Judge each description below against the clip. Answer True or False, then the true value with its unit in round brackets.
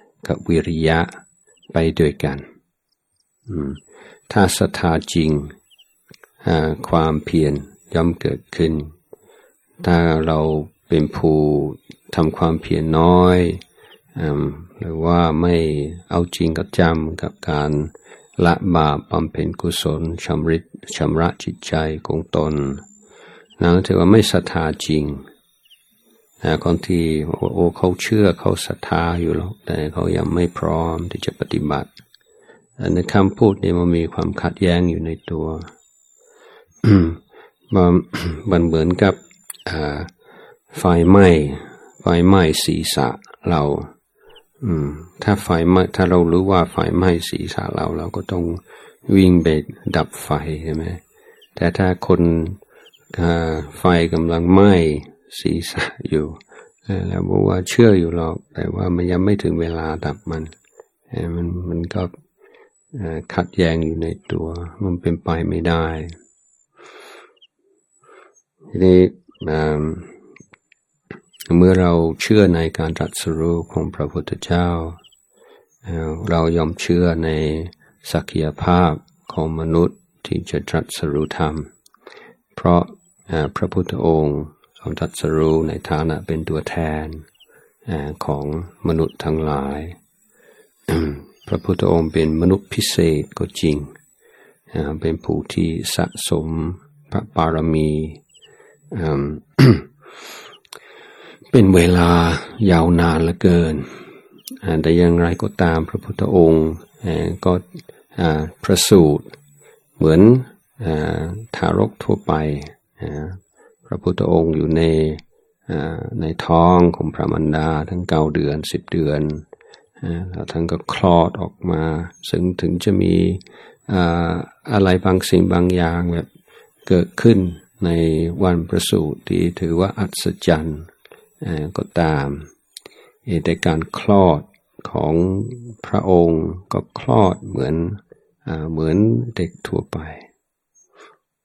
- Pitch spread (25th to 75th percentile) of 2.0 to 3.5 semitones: True (2.5 semitones)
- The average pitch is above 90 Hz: False (85 Hz)